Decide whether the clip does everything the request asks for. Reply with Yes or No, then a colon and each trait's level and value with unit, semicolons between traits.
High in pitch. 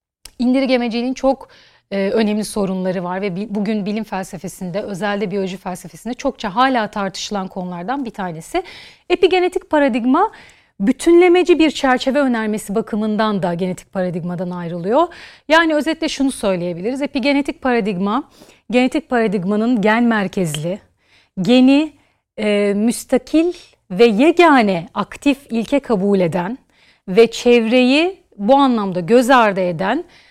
Yes: high, 225 Hz